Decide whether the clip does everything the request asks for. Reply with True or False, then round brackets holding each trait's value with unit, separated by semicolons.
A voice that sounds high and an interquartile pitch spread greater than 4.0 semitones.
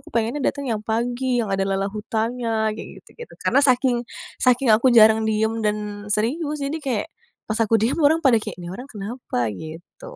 False (230 Hz; 3.5 semitones)